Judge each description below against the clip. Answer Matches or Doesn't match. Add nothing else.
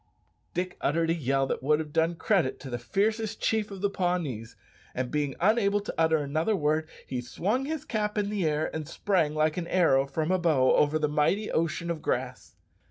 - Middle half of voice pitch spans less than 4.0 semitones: Doesn't match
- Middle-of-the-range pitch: Matches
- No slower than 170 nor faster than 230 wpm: Matches